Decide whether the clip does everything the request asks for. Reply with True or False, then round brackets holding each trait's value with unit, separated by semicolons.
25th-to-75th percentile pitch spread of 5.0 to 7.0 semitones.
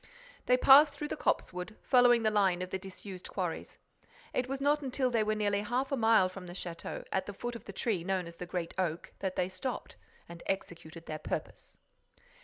True (5.3 semitones)